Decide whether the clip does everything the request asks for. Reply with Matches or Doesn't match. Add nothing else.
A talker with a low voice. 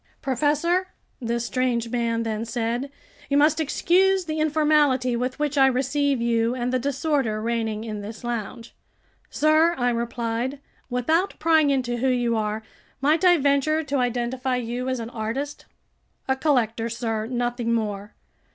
Doesn't match